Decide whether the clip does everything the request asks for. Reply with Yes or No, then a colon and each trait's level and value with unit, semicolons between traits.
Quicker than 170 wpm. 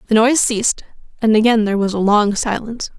Yes: average, 200 wpm